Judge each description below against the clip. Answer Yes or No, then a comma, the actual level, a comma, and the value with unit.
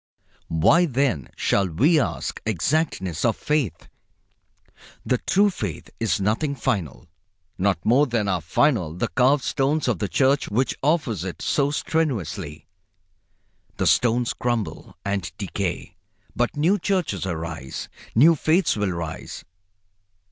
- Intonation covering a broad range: Yes, wide, 8.0 semitones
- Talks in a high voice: No, low, 115 Hz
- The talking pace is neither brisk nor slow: No, slow, 125 wpm